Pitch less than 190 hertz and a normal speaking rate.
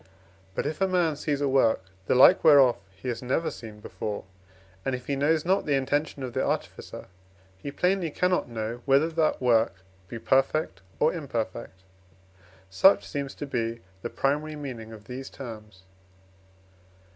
Yes: low, 135 Hz; average, 160 wpm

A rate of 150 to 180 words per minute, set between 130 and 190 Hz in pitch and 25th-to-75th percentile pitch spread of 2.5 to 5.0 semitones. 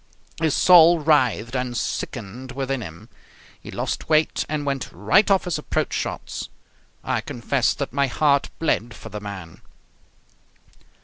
No: average, 140 wpm; low, 135 Hz; average, 4.5 semitones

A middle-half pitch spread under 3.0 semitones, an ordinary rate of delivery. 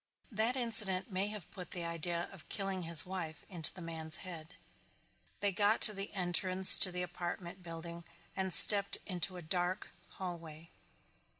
Yes: narrow, 2.4 semitones; average, 160 wpm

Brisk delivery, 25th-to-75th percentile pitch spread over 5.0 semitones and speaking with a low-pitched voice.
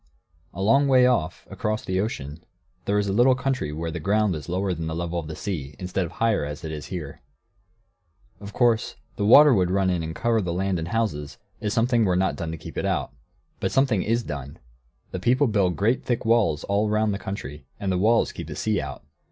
Yes: fast, 230 wpm; wide, 5.4 semitones; very low, 95 Hz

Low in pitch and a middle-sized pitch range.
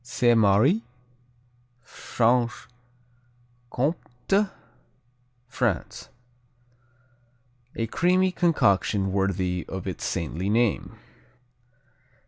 No: low, 115 Hz; wide, 5.8 semitones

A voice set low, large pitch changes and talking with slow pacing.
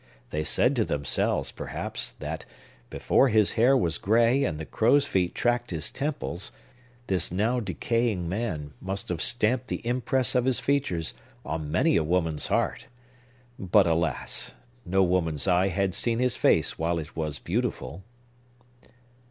No: very low, 95 Hz; wide, 6.6 semitones; average, 150 wpm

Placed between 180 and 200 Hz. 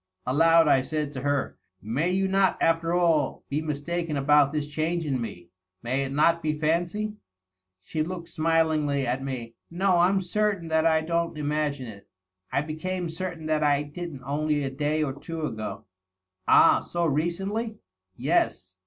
No: medium, 155 Hz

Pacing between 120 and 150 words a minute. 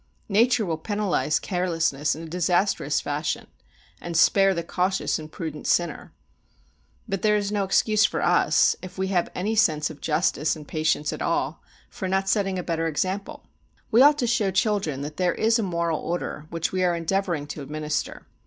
No: average, 180 wpm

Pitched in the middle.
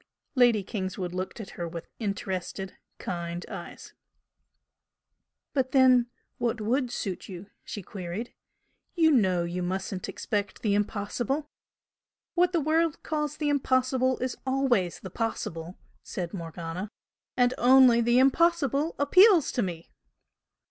No: high, 230 Hz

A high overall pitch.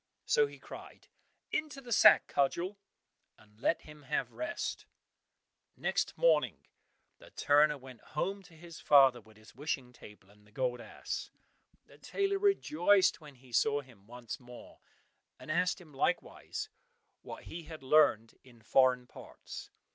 No: medium, 145 Hz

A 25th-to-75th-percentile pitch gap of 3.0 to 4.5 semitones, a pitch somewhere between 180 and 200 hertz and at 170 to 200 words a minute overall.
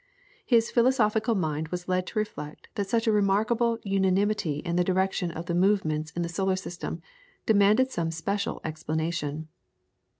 No: average, 4.0 semitones; high, 190 Hz; average, 155 wpm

